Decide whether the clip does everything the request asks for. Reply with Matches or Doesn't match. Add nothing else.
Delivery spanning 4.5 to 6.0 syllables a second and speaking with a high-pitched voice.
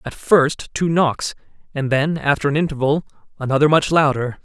Doesn't match